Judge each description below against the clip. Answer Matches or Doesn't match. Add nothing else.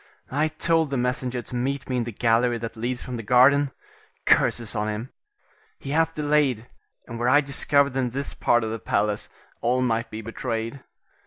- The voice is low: Matches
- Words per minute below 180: Doesn't match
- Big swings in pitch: Doesn't match